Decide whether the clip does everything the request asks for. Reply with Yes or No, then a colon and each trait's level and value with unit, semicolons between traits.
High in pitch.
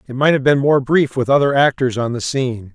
No: low, 135 Hz